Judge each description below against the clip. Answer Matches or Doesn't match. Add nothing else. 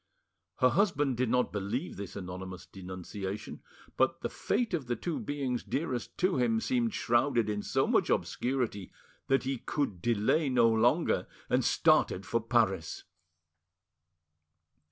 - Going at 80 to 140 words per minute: Matches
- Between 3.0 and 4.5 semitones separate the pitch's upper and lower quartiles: Doesn't match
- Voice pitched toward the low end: Matches